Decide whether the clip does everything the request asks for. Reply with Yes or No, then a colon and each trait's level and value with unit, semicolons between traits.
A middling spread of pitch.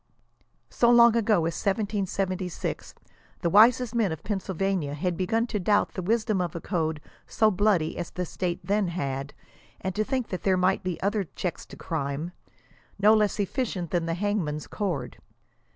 Yes: average, 3.7 semitones